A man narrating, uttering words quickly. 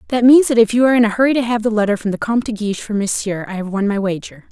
No: female; fast, 330 wpm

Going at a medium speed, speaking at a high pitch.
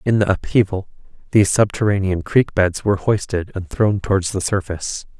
No: average, 160 wpm; low, 100 Hz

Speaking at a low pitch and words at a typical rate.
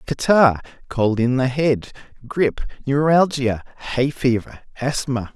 No: low, 130 Hz; slow, 110 wpm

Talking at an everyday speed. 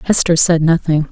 Yes: average, 160 wpm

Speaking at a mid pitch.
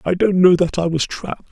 Yes: medium, 175 Hz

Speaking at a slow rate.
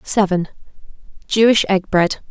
Yes: slow, 80 wpm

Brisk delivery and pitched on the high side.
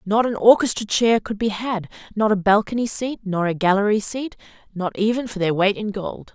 Yes: fast, 210 wpm; high, 210 Hz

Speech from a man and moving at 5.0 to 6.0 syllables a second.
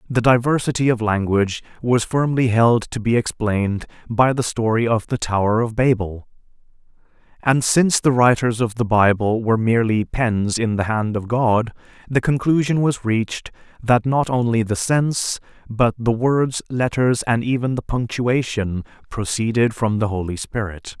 No: male; 4.7 syllables/s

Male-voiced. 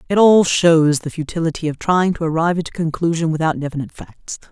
No: female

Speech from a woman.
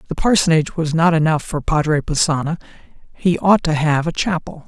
No: male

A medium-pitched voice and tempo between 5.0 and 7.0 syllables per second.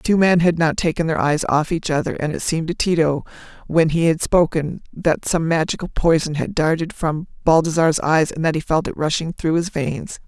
Yes: medium, 160 Hz; 5.4 syllables/s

